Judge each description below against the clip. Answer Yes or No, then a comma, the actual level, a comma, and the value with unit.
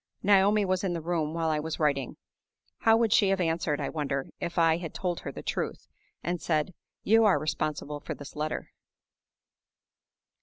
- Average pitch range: Yes, average, 3.7 semitones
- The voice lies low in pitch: No, medium, 165 Hz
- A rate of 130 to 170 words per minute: No, average, 180 wpm